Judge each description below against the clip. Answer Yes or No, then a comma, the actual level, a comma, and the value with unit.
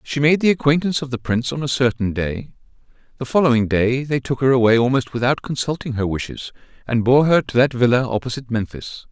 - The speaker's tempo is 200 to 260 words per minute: Yes, fast, 205 wpm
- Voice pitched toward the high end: No, low, 130 Hz